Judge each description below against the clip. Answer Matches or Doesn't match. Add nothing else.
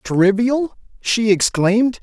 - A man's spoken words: Matches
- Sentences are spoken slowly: Matches